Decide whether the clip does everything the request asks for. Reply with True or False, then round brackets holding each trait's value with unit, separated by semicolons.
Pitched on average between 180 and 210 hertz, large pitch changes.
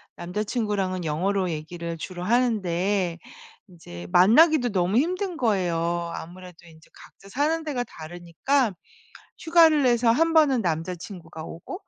True (190 Hz; 6.5 semitones)